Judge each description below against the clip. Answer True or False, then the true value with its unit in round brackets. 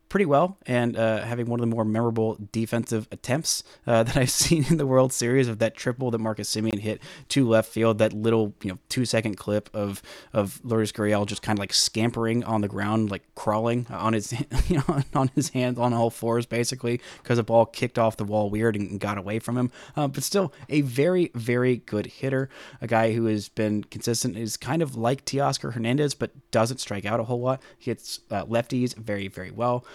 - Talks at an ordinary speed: False (220 wpm)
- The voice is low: True (115 Hz)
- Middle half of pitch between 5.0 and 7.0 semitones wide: False (3.0 semitones)